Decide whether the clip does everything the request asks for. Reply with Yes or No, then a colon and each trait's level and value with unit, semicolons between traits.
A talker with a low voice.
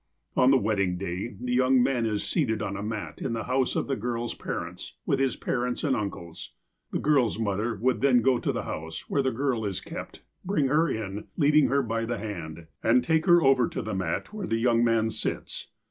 Yes: low, 120 Hz